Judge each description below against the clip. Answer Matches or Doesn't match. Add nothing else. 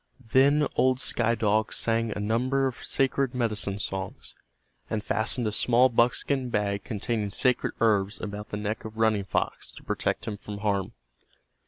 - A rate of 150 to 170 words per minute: Matches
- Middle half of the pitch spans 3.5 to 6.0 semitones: Doesn't match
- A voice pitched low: Matches